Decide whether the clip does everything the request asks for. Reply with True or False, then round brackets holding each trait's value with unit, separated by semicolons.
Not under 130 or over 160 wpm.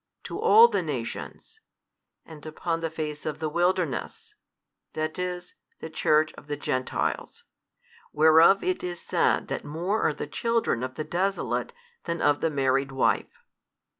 True (150 wpm)